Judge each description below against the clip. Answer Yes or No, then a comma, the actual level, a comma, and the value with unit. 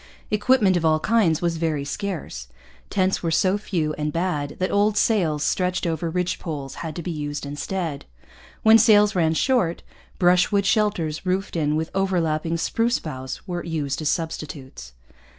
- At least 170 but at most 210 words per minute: No, average, 160 wpm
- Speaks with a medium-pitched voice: Yes, medium, 170 Hz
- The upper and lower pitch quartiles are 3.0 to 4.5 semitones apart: Yes, average, 4.0 semitones